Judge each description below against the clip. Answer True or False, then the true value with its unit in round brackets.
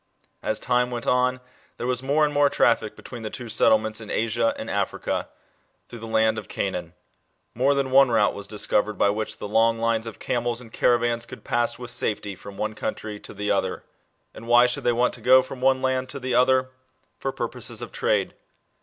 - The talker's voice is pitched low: True (120 Hz)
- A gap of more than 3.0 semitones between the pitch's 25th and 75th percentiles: False (2.7 semitones)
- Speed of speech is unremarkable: False (210 wpm)